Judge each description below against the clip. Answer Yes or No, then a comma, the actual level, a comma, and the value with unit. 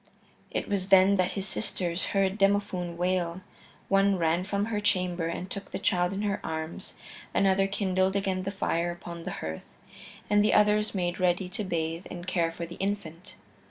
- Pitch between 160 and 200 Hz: Yes, medium, 185 Hz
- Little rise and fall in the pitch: Yes, narrow, 2.3 semitones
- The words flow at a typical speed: Yes, average, 180 wpm